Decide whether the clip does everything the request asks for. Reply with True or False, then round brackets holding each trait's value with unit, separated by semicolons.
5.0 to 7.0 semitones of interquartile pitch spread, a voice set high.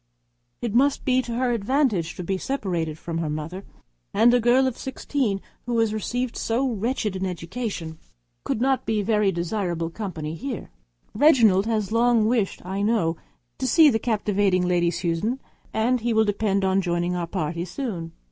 True (5.3 semitones; 210 Hz)